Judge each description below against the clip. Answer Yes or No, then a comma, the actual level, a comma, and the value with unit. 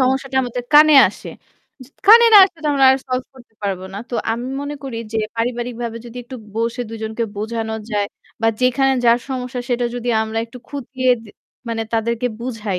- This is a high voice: Yes, high, 240 Hz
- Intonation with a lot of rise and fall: No, narrow, 2.5 semitones